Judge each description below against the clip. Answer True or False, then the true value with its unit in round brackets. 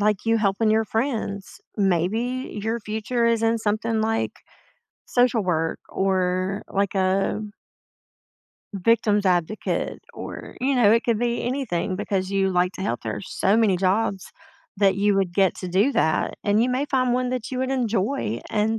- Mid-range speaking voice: False (210 Hz)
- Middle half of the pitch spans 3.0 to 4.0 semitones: True (3.4 semitones)